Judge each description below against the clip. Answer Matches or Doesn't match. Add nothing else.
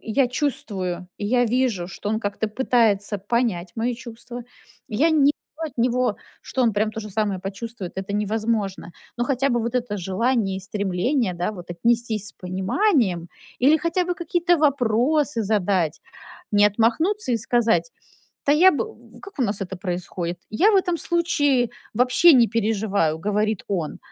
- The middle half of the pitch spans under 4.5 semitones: Doesn't match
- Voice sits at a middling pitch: Doesn't match